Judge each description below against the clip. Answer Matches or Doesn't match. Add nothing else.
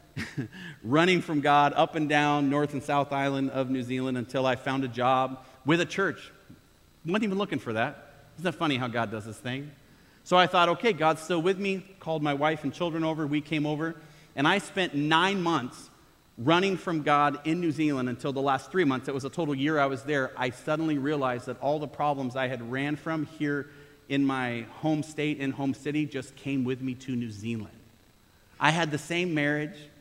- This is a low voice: Doesn't match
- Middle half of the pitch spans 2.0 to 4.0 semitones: Matches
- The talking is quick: Matches